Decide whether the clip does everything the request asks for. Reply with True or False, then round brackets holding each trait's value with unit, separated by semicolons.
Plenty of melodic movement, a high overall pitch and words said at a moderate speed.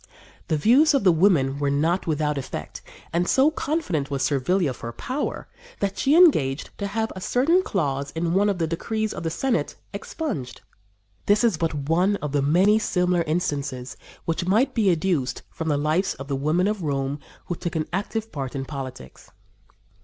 False (6.4 semitones; 170 Hz; 185 wpm)